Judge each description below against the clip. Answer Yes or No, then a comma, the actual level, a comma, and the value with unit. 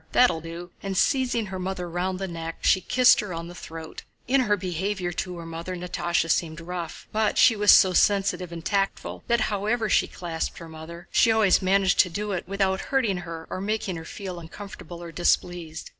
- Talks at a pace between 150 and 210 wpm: Yes, average, 200 wpm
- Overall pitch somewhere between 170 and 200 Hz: Yes, medium, 185 Hz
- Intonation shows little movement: No, average, 3.1 semitones